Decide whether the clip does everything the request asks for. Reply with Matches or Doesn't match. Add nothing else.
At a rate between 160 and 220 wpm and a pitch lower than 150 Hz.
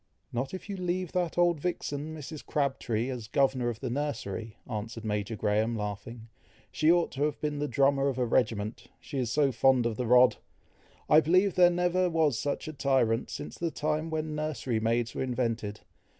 Matches